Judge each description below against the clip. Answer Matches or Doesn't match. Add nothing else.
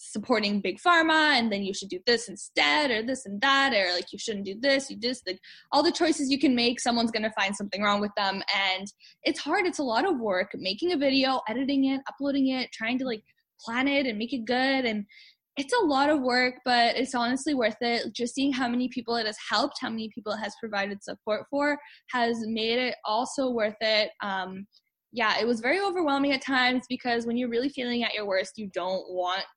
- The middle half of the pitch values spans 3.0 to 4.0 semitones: Doesn't match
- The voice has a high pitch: Matches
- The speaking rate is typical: Doesn't match